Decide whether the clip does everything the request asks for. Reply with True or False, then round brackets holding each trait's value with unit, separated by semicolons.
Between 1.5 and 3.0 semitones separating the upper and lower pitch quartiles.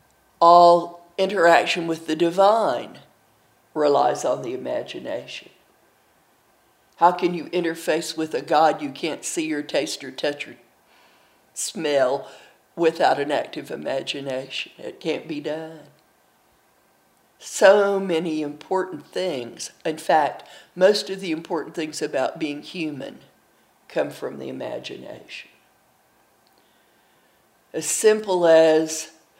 True (2.6 semitones)